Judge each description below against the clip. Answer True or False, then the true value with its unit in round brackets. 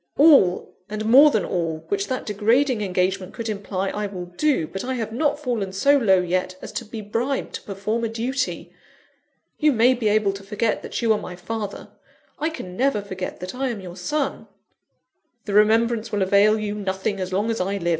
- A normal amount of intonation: True (4.1 semitones)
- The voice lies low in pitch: False (210 Hz)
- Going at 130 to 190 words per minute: False (205 wpm)